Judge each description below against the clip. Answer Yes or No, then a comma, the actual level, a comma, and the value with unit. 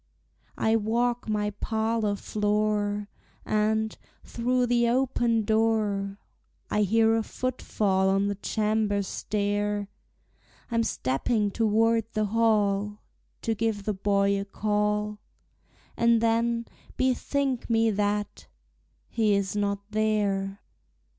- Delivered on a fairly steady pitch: Yes, narrow, 1.8 semitones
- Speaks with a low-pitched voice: No, high, 215 Hz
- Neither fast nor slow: No, slow, 110 wpm